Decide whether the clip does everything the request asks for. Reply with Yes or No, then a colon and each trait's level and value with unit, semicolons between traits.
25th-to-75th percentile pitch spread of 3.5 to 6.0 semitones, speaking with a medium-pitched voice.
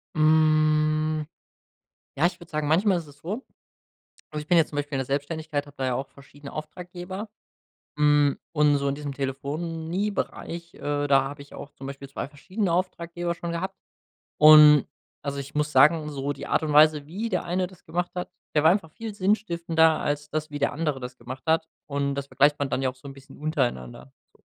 No: average, 3.1 semitones; medium, 150 Hz